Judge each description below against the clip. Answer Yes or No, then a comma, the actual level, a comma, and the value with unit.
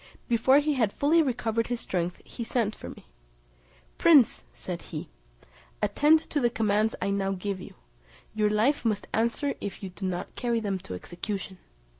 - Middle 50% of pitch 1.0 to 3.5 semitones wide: No, average, 3.9 semitones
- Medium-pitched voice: No, high, 220 Hz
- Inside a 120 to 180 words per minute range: Yes, average, 170 wpm